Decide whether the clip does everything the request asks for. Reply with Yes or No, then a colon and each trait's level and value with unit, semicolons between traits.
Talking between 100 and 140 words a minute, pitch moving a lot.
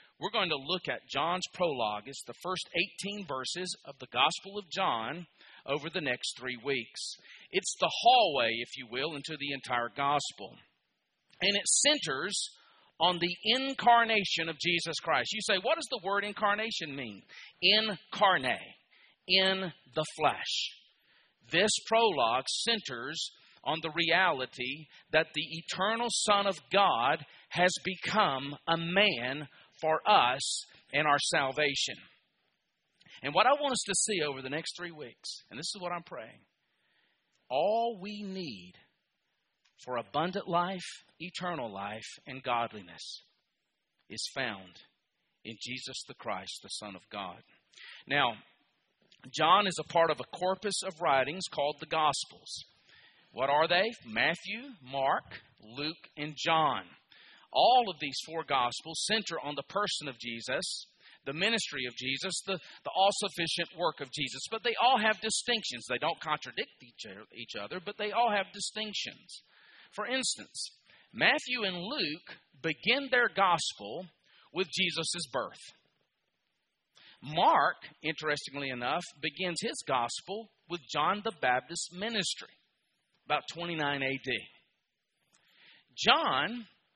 Yes: slow, 135 wpm; wide, 6.1 semitones